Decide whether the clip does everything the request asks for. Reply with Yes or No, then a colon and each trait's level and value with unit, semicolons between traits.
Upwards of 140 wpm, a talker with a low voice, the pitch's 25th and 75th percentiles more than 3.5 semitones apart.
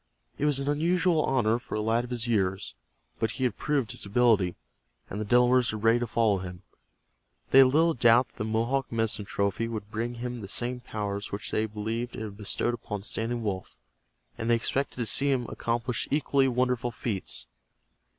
No: average, 195 wpm; low, 115 Hz; average, 2.8 semitones